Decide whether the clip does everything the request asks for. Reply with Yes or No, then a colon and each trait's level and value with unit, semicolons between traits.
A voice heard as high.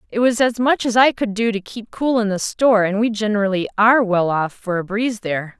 Yes: high, 215 Hz